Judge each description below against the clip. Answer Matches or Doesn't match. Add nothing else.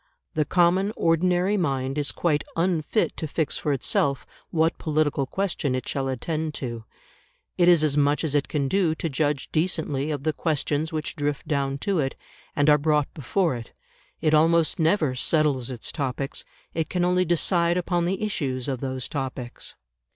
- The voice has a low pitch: Doesn't match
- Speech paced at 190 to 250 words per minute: Doesn't match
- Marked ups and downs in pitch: Doesn't match